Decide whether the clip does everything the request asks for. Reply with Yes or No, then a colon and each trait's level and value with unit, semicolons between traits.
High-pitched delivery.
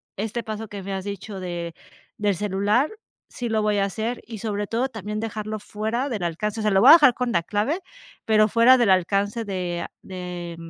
Yes: high, 210 Hz